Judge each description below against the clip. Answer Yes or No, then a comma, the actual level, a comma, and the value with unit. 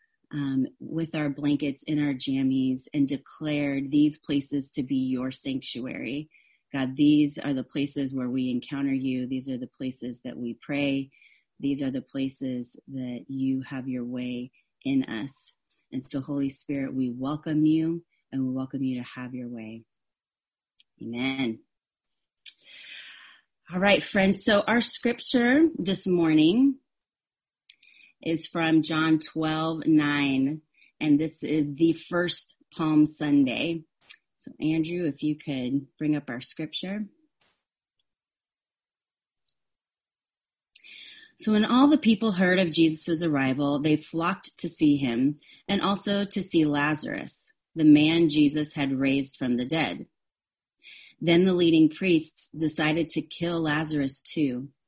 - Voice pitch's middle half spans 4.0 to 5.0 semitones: No, average, 3.6 semitones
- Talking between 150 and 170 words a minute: No, slow, 135 wpm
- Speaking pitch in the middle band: Yes, medium, 150 Hz